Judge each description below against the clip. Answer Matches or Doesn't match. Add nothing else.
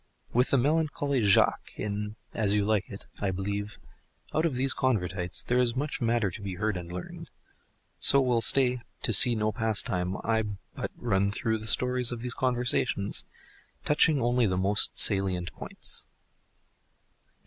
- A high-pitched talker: Doesn't match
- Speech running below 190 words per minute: Matches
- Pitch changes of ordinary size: Matches